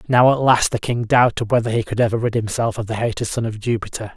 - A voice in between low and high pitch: No, low, 115 Hz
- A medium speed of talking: No, fast, 260 wpm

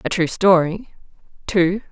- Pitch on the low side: No, medium, 180 Hz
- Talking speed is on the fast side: No, slow, 125 wpm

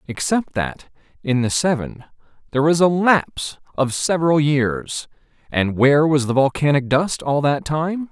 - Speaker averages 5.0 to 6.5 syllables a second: No, 4.6 syllables/s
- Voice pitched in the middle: Yes, medium, 145 Hz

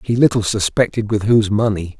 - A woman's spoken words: No, male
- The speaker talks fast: No, average, 180 wpm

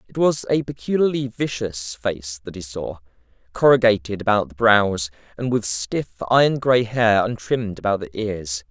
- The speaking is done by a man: Yes, male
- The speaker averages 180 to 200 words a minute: No, average, 160 wpm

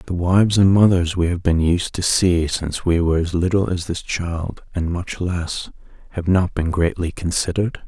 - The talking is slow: No, average, 200 wpm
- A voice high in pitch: No, very low, 90 Hz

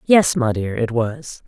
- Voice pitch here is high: No, medium, 160 Hz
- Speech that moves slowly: No, fast, 205 wpm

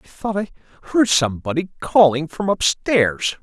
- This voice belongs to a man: Yes, male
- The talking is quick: No, average, 140 wpm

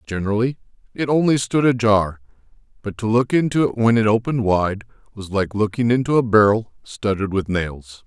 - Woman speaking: No, male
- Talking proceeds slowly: No, average, 170 wpm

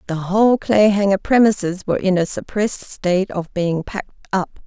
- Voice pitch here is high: Yes, high, 195 Hz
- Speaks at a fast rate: No, average, 165 wpm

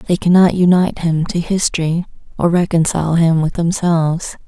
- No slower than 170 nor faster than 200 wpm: No, average, 145 wpm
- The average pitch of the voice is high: No, medium, 170 Hz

